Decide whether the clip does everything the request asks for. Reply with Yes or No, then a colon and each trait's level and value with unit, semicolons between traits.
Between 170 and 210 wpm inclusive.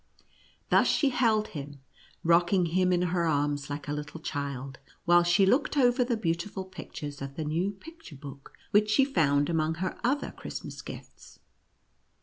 No: average, 160 wpm